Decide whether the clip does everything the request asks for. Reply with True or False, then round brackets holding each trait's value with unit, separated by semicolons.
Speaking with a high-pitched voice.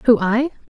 True (240 Hz)